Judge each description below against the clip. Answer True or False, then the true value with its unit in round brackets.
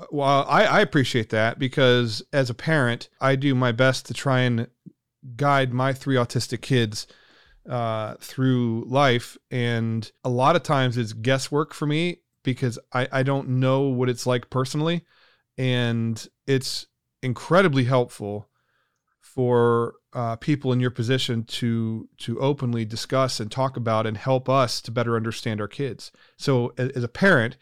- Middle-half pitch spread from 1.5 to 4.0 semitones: True (2.4 semitones)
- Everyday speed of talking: True (155 wpm)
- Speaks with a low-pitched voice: True (125 Hz)